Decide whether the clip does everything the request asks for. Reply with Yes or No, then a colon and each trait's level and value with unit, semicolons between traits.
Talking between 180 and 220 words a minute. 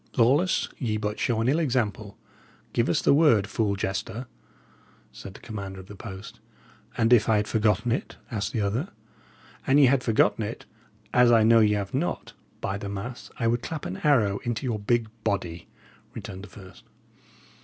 Yes: average, 185 wpm